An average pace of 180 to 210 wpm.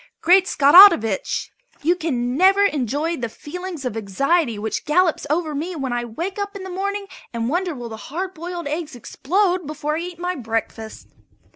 No: average, 170 wpm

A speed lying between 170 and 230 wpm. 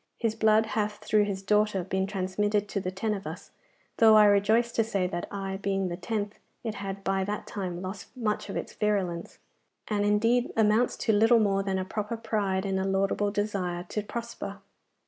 Yes: average, 195 wpm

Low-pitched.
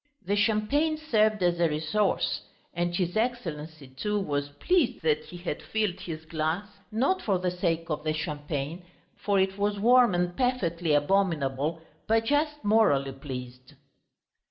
No: medium, 175 Hz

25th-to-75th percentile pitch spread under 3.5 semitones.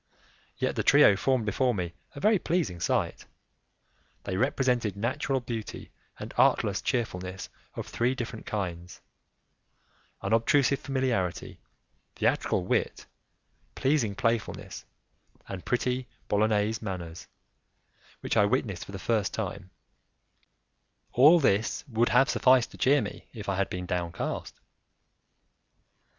No: average, 5.1 semitones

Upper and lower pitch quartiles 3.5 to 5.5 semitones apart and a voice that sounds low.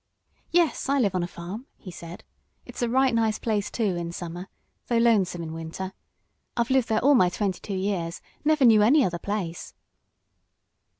No: average, 5.2 semitones; high, 205 Hz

